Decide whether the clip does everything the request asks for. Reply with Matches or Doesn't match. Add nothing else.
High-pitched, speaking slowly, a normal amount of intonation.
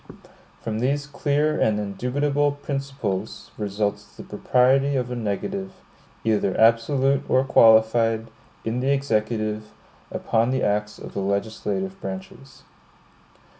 Doesn't match